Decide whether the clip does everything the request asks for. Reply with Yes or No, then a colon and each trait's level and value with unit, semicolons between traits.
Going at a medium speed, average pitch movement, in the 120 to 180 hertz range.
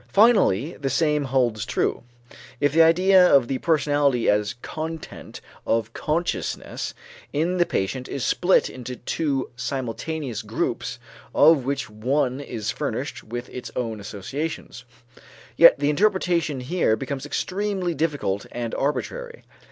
No: slow, 130 wpm; average, 5.0 semitones; medium, 140 Hz